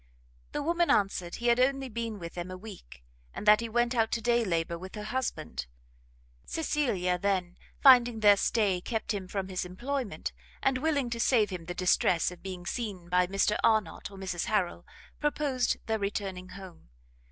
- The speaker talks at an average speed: Yes, average, 180 wpm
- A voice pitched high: Yes, high, 205 Hz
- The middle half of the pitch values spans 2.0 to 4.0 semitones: No, average, 4.7 semitones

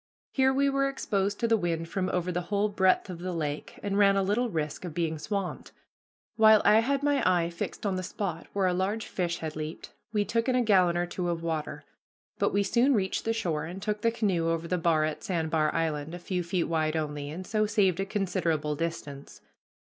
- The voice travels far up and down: No, average, 4.0 semitones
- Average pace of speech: No, fast, 225 wpm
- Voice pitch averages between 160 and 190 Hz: Yes, medium, 185 Hz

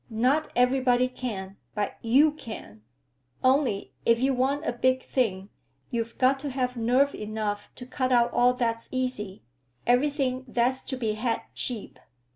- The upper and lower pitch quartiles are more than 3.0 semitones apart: No, narrow, 2.4 semitones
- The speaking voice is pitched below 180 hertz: No, very high, 250 Hz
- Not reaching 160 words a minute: Yes, average, 150 wpm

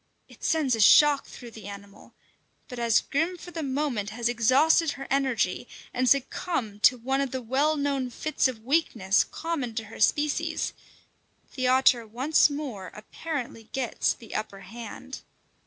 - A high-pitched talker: Yes, very high, 255 Hz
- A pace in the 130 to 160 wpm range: Yes, average, 155 wpm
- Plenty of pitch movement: No, average, 4.1 semitones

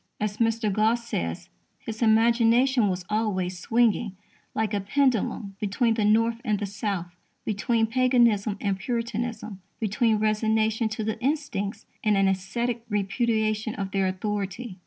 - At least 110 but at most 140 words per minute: Yes, slow, 135 wpm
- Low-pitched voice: No, high, 215 Hz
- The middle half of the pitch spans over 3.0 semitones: No, narrow, 2.5 semitones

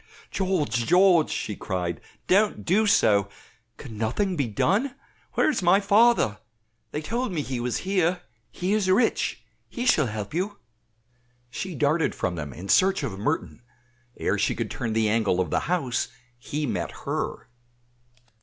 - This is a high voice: No, medium, 155 Hz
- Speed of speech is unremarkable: Yes, average, 155 wpm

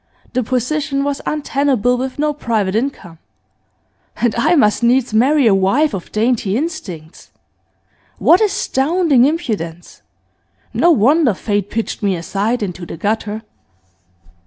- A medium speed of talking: No, slow, 125 wpm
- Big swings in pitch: Yes, wide, 5.8 semitones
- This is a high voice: Yes, high, 240 Hz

